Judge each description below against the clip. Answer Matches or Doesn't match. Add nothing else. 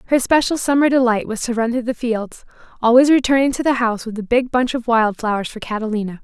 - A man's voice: Doesn't match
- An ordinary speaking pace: Doesn't match